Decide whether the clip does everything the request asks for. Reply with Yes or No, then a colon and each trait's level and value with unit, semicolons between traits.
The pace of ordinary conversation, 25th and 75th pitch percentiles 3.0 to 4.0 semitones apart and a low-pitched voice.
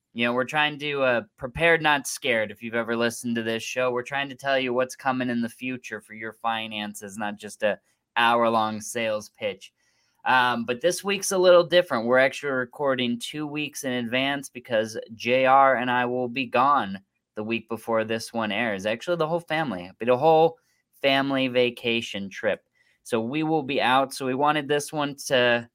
Yes: average, 195 wpm; average, 3.4 semitones; low, 125 Hz